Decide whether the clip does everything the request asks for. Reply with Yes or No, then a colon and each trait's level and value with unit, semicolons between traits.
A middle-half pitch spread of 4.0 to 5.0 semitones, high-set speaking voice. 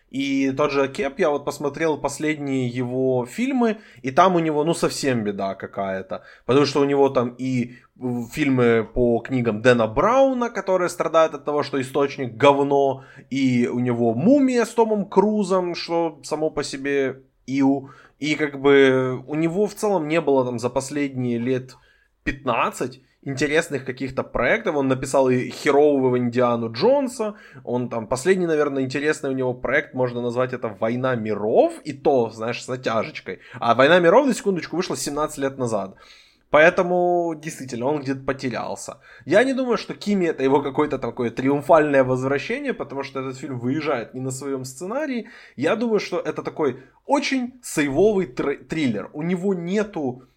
No: average, 4.6 semitones; medium, 140 Hz